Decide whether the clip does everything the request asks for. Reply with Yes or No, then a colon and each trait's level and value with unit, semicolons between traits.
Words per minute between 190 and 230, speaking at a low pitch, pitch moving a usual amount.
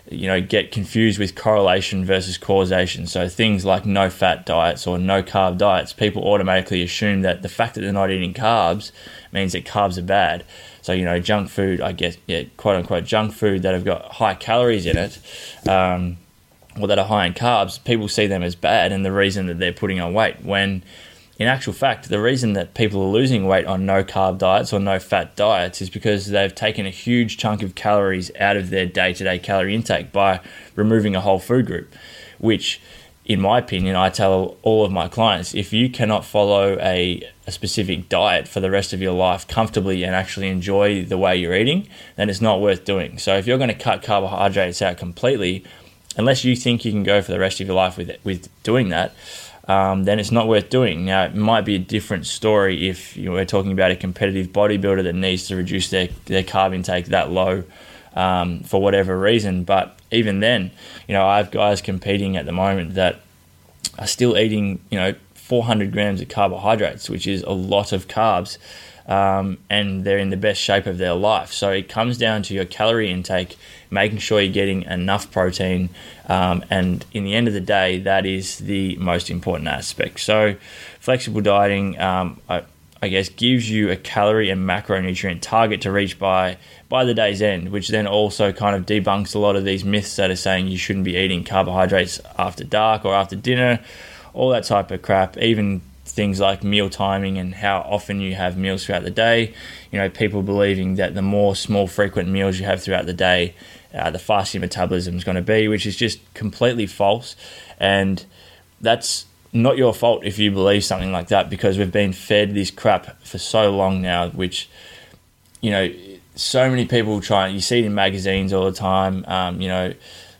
No: fast, 205 wpm; very low, 95 Hz; narrow, 2.0 semitones